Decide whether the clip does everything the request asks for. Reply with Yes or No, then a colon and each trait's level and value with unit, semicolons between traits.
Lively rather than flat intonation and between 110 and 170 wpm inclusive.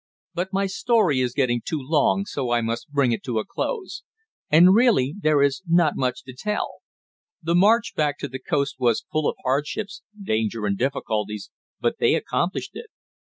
No: wide, 6.3 semitones; average, 180 wpm